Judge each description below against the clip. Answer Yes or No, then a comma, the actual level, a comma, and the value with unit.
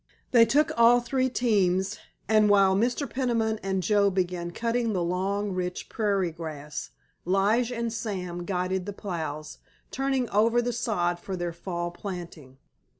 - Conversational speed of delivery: Yes, average, 150 wpm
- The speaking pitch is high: Yes, high, 195 Hz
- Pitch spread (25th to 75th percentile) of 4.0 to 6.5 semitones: Yes, average, 4.6 semitones